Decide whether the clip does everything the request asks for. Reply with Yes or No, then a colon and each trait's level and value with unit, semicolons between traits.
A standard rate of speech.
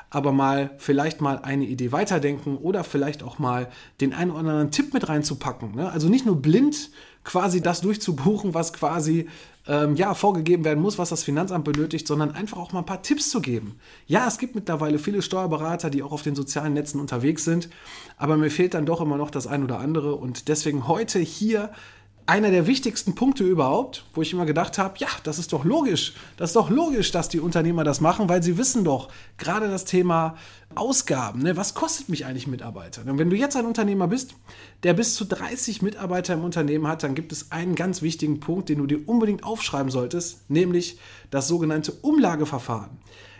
No: fast, 200 wpm